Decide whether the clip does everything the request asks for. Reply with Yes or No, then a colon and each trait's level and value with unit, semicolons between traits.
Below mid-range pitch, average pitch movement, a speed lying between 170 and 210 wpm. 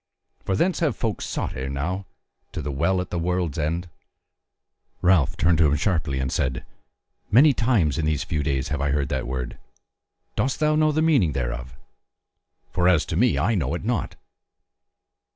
No: very low, 85 Hz; wide, 6.4 semitones; average, 180 wpm